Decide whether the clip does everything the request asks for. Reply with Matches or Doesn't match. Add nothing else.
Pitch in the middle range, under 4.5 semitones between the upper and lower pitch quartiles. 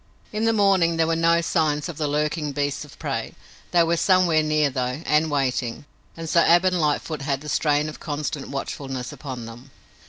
Matches